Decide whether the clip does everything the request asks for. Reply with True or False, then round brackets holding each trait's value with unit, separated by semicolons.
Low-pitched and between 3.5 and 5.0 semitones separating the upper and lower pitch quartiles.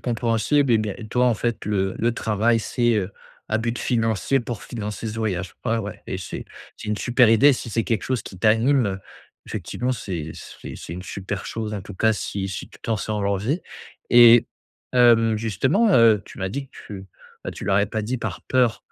False (110 Hz; 2.9 semitones)